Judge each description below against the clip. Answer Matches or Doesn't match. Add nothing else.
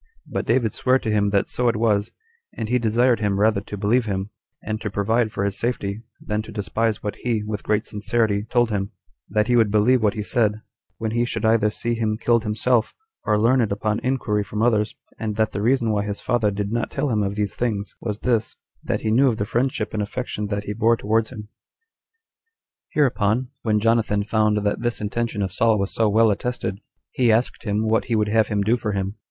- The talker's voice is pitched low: Matches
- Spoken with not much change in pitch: Matches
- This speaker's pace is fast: Matches